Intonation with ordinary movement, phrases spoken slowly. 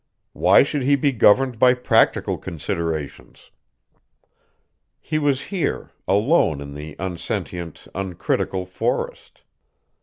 No: wide, 8.2 semitones; slow, 100 wpm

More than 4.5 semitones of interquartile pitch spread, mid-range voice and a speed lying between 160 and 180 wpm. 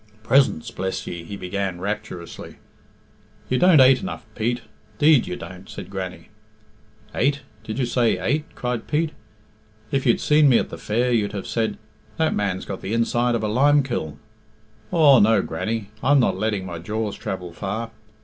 No: average, 5.3 semitones; low, 110 Hz; average, 170 wpm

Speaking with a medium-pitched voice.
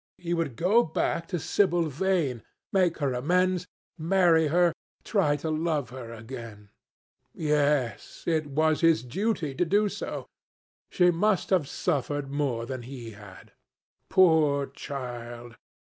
Yes: medium, 150 Hz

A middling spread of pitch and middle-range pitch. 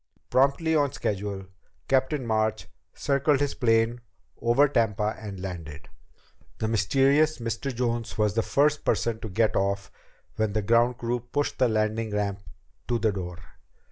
No: average, 4.1 semitones; low, 115 Hz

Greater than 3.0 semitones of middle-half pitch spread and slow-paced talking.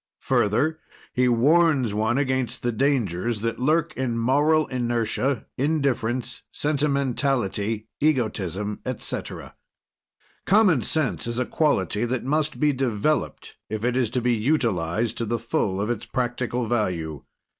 Yes: average, 4.0 semitones; slow, 130 wpm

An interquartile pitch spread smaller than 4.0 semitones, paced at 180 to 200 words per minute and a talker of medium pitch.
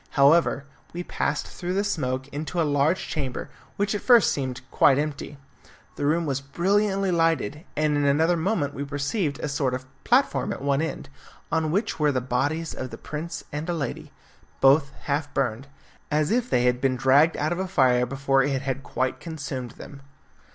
Yes: average, 3.6 semitones; average, 185 wpm; medium, 145 Hz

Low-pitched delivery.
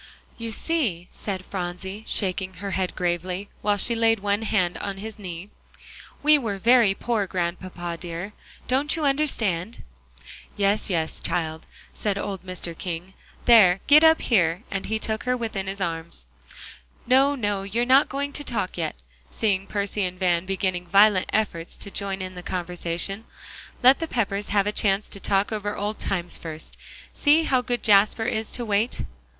No: high, 200 Hz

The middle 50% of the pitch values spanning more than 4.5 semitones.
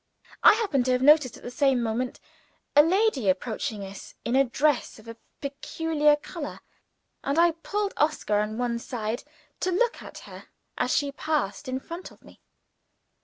Yes: average, 5.0 semitones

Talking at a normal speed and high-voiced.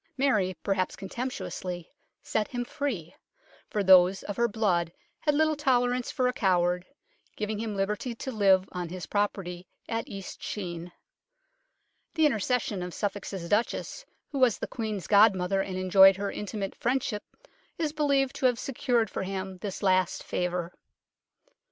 Yes: average, 145 wpm; high, 205 Hz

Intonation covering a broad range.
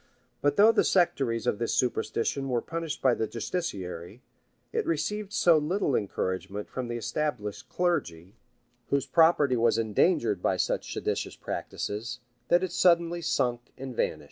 Yes: wide, 7.0 semitones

